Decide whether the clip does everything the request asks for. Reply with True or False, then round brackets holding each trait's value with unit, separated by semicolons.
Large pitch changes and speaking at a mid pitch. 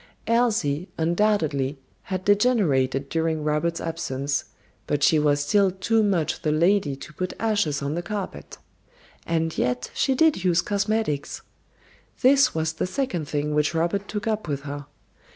True (5.7 semitones; 165 Hz)